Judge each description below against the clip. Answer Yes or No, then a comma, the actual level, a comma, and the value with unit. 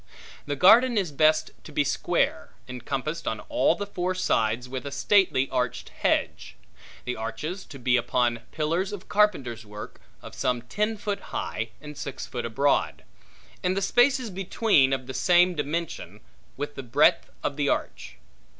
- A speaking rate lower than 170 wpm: Yes, average, 160 wpm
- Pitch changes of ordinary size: No, wide, 6.8 semitones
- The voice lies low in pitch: No, medium, 145 Hz